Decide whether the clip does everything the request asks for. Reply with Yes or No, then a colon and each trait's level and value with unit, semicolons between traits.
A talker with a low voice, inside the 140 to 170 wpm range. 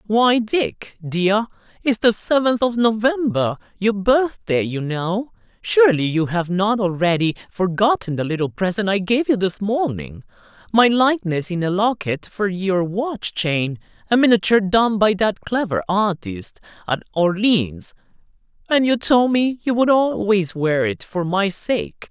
No: high, 200 Hz; average, 150 wpm